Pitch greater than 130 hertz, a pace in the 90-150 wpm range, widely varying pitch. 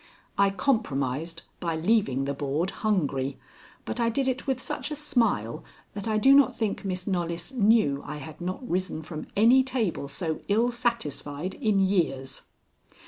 No: high, 190 Hz; average, 160 wpm; wide, 7.2 semitones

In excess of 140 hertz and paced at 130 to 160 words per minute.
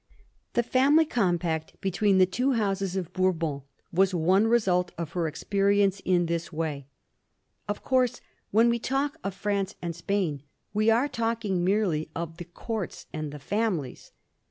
Yes: high, 190 Hz; average, 155 wpm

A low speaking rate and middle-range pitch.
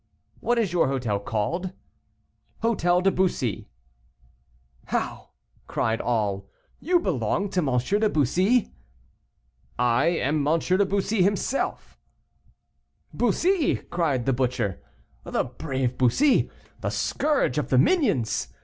Yes: slow, 115 wpm; medium, 165 Hz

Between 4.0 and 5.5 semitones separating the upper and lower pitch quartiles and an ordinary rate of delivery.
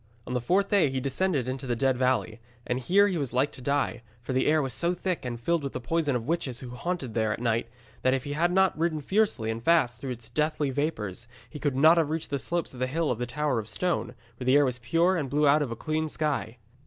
No: average, 4.7 semitones; fast, 265 wpm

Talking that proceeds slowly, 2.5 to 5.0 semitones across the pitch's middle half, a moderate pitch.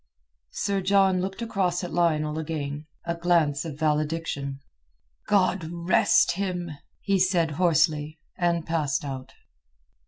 Yes: slow, 115 wpm; average, 3.3 semitones; medium, 170 Hz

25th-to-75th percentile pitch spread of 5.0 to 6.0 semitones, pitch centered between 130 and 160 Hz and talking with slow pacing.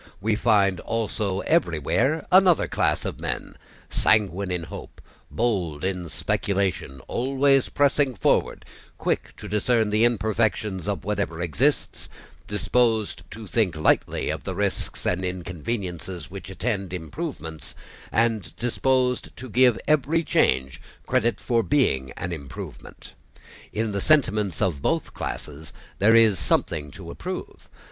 No: average, 5.3 semitones; low, 105 Hz; slow, 125 wpm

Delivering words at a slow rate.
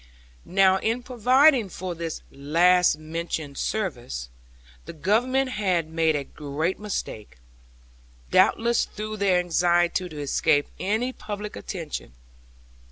Yes: slow, 110 wpm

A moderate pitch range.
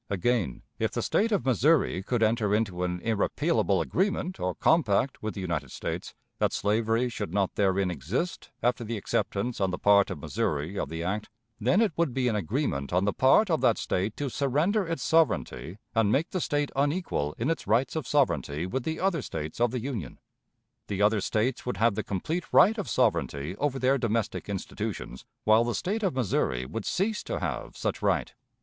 No: wide, 7.0 semitones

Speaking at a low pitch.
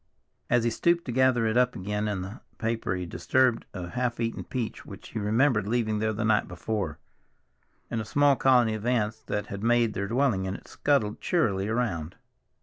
Yes: low, 110 Hz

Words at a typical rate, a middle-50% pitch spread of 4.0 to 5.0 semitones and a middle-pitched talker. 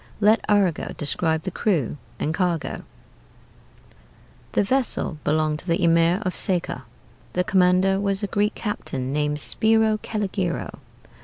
No: slow, 130 wpm; average, 4.4 semitones; medium, 180 Hz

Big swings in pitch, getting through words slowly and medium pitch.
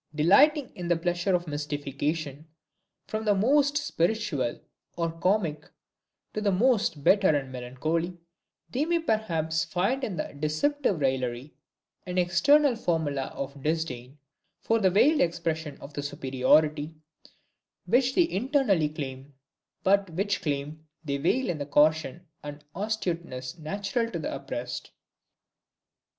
Yes: wide, 6.4 semitones; slow, 130 wpm; medium, 165 Hz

